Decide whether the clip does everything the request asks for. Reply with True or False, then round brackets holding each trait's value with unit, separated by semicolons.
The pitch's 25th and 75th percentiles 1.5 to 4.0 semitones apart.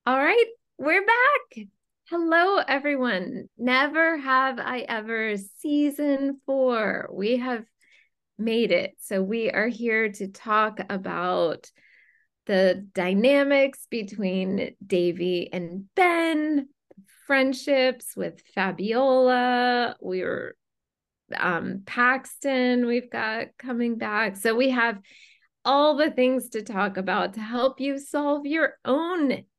False (4.7 semitones)